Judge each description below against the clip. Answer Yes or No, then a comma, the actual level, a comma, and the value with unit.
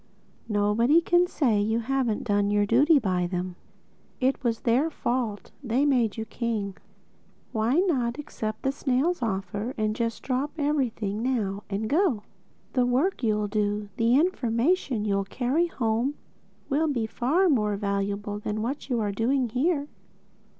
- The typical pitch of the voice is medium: No, high, 235 Hz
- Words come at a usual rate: Yes, average, 150 wpm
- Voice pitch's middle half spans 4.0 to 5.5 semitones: Yes, average, 4.6 semitones